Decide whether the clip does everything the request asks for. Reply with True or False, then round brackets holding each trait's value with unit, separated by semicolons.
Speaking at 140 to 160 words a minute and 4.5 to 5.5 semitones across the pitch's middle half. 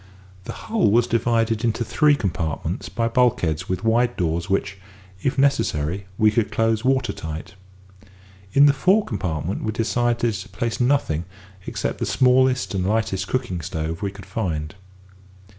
True (150 wpm; 5.0 semitones)